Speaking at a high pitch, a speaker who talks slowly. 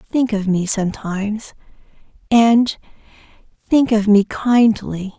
Yes: high, 215 Hz; slow, 95 wpm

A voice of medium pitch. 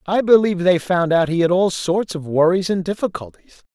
Yes: medium, 180 Hz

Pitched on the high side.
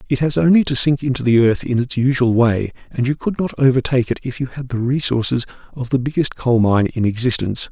No: low, 125 Hz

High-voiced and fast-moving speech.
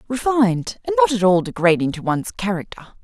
No: high, 195 Hz; average, 180 wpm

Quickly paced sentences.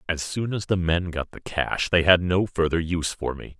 Yes: fast, 250 wpm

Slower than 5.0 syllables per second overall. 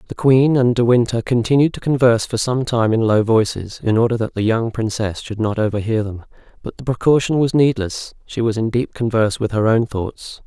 No: 5.4 syllables/s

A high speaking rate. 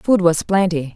No: average, 190 wpm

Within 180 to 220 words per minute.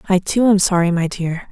No: fast, 240 wpm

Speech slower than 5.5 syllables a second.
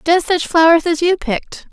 Yes: 5.1 syllables/s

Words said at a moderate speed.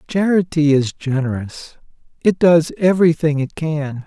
No: slow, 120 wpm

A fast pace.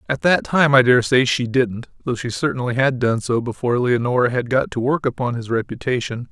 Yes: fast, 210 wpm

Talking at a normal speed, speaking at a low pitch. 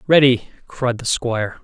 Yes: average, 145 wpm; low, 125 Hz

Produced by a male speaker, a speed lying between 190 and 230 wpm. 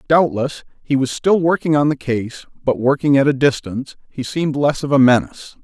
Yes: male; average, 200 wpm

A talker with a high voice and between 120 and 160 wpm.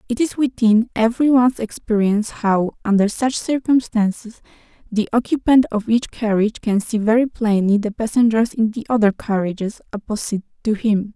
Yes: high, 220 Hz; average, 150 wpm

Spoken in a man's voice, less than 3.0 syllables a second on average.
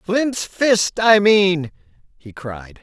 Yes: male; 2.6 syllables/s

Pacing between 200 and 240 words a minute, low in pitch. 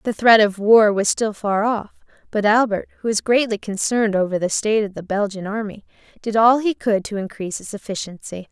No: fast, 205 wpm; high, 210 Hz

